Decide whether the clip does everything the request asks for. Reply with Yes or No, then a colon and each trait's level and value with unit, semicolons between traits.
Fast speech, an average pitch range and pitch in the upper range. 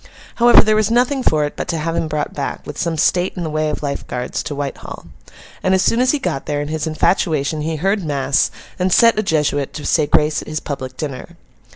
No: fast, 240 wpm; average, 4.2 semitones; medium, 155 Hz